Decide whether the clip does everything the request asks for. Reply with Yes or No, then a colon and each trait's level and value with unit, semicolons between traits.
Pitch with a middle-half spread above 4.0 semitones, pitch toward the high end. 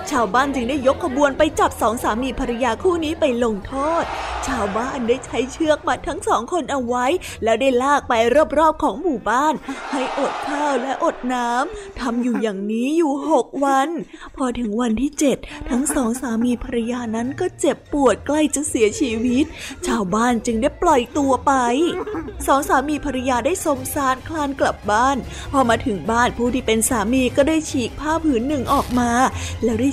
No: average, 3.7 semitones; very high, 270 Hz